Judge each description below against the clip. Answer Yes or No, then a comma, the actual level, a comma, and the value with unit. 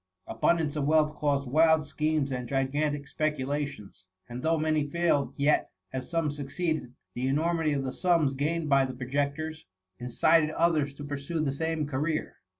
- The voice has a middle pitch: Yes, medium, 145 Hz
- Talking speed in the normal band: Yes, average, 160 wpm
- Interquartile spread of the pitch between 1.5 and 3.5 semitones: Yes, narrow, 2.4 semitones